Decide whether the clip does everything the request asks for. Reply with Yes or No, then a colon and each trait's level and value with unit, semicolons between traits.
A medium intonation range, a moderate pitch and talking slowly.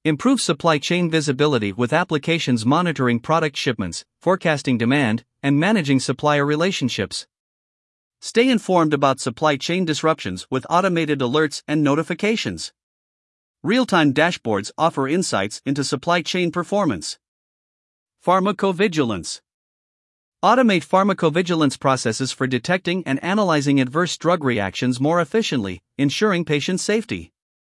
Yes: average, 4.6 semitones; medium, 155 Hz; slow, 110 wpm